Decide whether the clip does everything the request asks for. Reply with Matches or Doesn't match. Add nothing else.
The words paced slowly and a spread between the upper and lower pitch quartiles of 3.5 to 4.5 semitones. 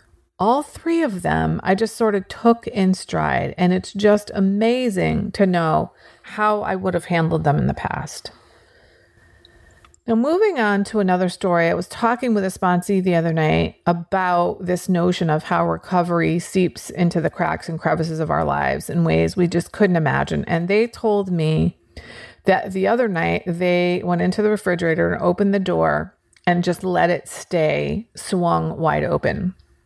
Doesn't match